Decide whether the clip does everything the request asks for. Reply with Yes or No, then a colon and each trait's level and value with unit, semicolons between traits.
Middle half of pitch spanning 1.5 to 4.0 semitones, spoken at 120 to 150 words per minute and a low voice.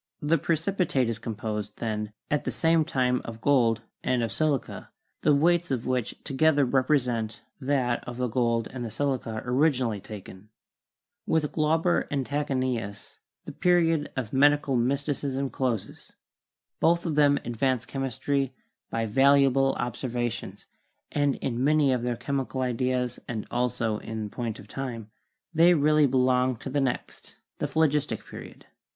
Yes: average, 3.5 semitones; average, 145 wpm; low, 130 Hz